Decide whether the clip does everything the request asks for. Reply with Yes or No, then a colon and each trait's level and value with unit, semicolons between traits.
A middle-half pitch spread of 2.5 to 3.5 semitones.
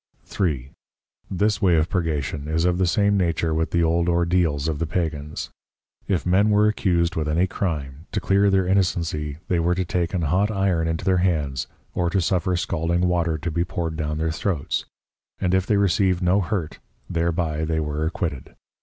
Yes: average, 2.8 semitones